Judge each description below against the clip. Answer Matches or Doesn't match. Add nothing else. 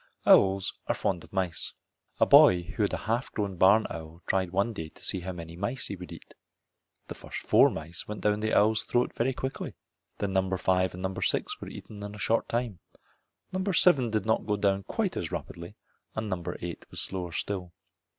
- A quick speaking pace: Matches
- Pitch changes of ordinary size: Matches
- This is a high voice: Doesn't match